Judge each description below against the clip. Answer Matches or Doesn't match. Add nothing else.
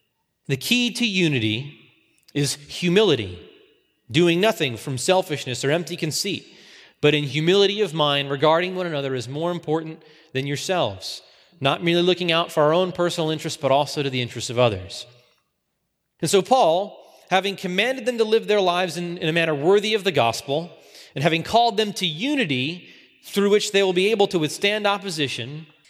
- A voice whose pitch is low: Doesn't match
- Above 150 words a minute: Matches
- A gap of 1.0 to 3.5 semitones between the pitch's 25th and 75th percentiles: Doesn't match